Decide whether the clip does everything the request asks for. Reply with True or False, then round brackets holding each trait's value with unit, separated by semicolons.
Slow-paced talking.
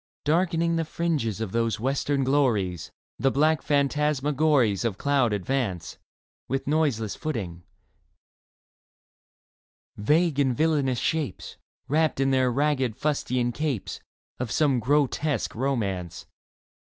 True (110 wpm)